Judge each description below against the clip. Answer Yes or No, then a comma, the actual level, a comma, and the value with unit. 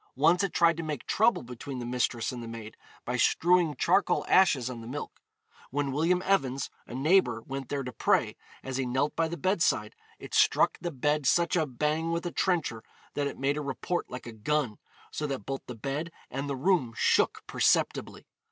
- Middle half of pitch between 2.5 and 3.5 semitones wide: No, average, 4.9 semitones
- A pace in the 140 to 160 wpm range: No, average, 200 wpm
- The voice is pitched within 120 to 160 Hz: Yes, medium, 140 Hz